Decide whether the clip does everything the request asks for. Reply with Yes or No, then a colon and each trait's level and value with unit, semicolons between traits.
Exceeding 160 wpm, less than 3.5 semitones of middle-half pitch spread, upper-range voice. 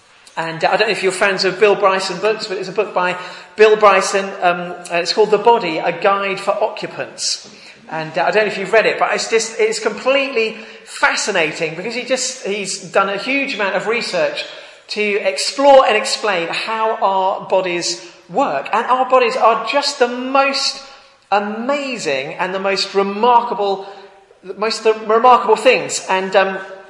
No: average, 175 wpm; average, 3.9 semitones; high, 205 Hz